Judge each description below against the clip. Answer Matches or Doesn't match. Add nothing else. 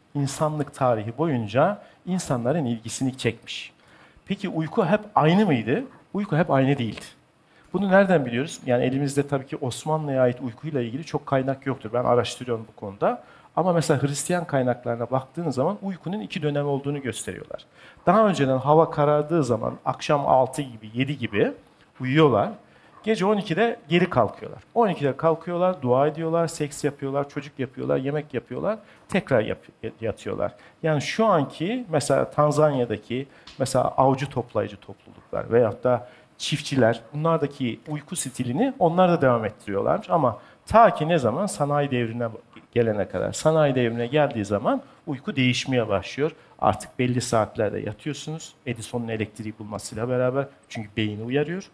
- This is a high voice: Doesn't match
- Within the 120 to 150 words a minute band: Matches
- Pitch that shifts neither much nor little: Matches